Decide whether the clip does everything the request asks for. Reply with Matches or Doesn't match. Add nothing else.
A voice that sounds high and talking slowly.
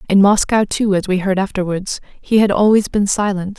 Doesn't match